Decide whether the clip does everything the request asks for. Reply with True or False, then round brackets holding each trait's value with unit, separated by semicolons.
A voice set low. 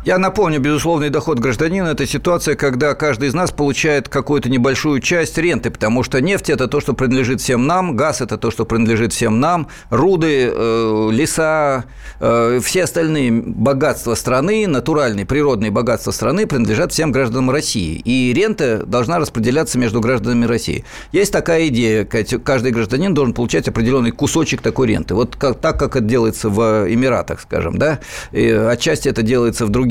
True (130 Hz)